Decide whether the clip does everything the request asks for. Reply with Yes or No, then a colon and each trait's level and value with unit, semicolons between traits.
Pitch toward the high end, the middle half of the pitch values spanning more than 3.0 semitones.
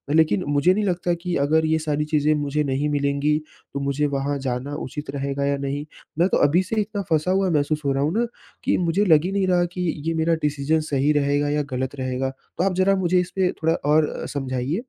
No: medium, 150 Hz; average, 3.7 semitones